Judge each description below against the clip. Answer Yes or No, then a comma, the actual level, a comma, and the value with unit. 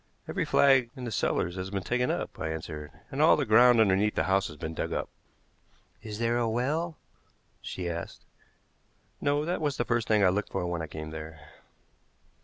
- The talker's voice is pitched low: Yes, low, 105 Hz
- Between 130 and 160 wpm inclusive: No, average, 200 wpm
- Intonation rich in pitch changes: Yes, wide, 6.1 semitones